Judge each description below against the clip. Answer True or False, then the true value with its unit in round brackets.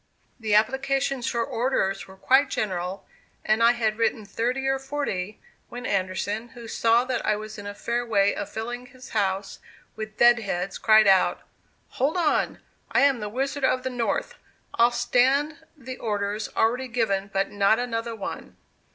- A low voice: False (230 Hz)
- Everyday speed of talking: True (170 wpm)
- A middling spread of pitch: True (3.7 semitones)